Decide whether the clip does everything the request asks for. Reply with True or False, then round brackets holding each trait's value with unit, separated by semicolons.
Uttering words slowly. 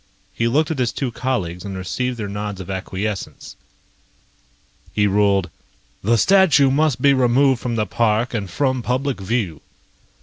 False (155 wpm)